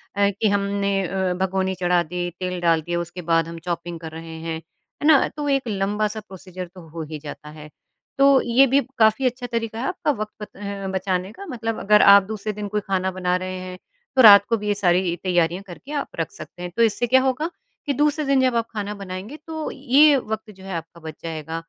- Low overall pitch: No, high, 200 Hz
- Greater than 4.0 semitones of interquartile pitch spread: Yes, average, 4.7 semitones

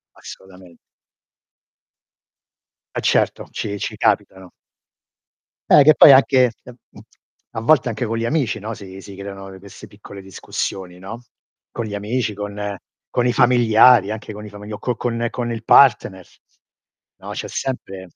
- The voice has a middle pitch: No, low, 110 Hz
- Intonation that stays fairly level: No, average, 3.8 semitones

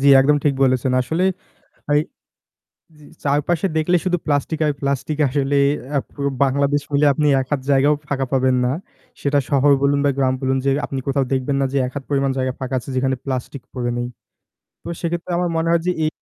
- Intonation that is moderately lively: No, narrow, 2.0 semitones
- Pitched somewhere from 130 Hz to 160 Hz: Yes, medium, 140 Hz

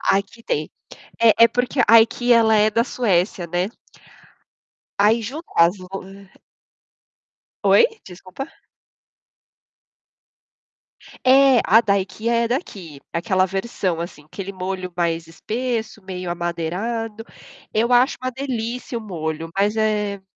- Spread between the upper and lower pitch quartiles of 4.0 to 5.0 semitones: Yes, average, 4.4 semitones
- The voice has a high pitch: Yes, high, 210 Hz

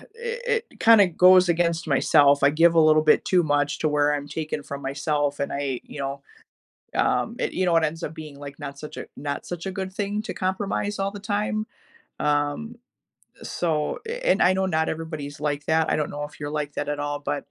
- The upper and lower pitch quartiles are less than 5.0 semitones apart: Yes, average, 4.4 semitones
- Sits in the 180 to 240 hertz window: No, medium, 155 Hz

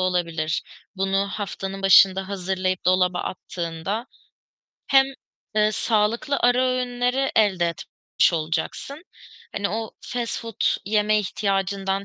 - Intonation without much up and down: No, average, 3.6 semitones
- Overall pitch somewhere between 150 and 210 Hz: Yes, high, 195 Hz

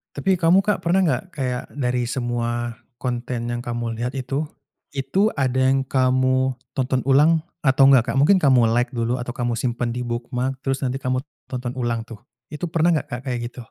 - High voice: No, low, 130 Hz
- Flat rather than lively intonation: Yes, narrow, 2.2 semitones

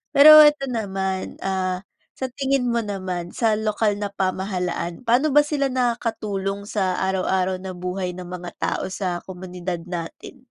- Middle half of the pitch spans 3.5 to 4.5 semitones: Yes, average, 4.2 semitones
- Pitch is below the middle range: No, high, 195 Hz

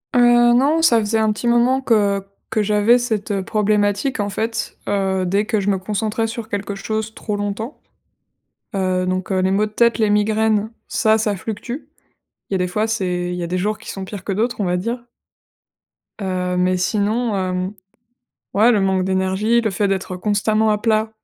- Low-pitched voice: No, high, 210 Hz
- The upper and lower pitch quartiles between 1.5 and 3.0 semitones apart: Yes, average, 2.7 semitones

